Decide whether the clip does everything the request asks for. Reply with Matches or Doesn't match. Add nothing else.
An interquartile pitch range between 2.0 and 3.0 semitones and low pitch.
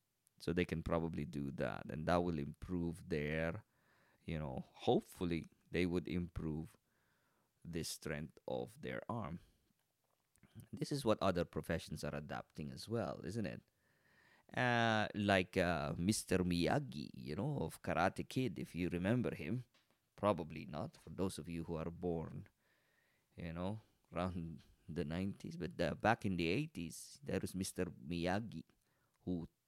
Doesn't match